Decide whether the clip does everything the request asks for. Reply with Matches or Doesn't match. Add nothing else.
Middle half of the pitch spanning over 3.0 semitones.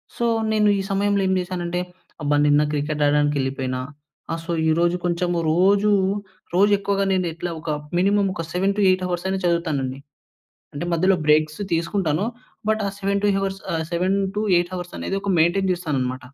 Matches